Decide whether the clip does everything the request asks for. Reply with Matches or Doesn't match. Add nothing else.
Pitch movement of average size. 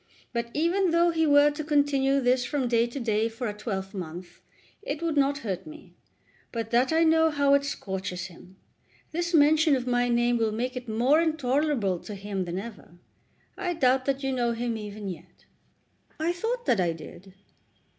Doesn't match